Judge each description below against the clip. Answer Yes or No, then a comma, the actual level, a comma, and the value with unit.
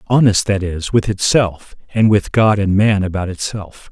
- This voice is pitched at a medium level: No, low, 100 Hz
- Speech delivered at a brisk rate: No, average, 185 wpm